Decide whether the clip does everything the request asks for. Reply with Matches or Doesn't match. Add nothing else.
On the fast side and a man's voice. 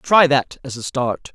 Doesn't match